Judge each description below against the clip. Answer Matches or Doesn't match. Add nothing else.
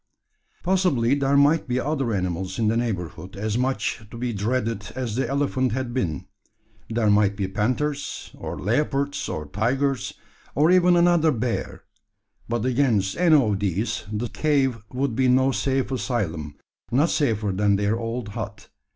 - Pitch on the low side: Matches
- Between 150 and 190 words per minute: Matches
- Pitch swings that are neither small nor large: Matches